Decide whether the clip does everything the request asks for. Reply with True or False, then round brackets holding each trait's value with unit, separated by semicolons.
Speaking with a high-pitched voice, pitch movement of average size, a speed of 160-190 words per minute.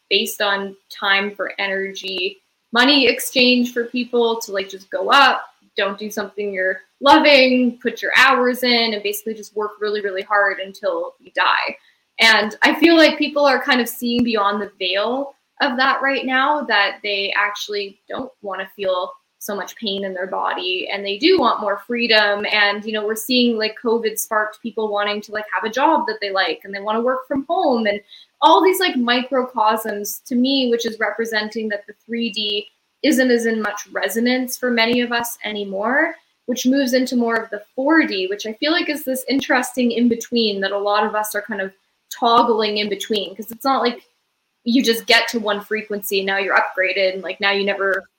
False (220 Hz; 3.7 semitones; 200 wpm)